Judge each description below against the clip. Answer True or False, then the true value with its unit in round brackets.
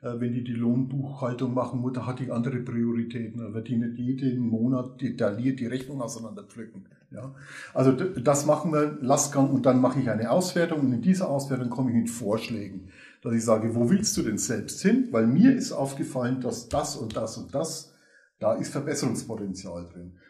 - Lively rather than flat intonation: False (2.8 semitones)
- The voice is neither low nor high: False (125 Hz)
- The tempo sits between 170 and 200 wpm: True (185 wpm)